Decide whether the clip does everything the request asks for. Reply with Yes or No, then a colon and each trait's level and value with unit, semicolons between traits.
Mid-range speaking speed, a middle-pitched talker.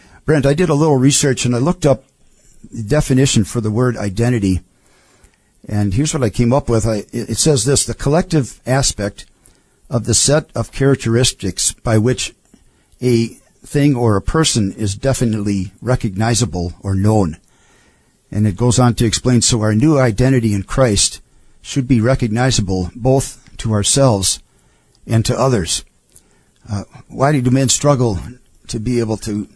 No: average, 155 wpm; low, 120 Hz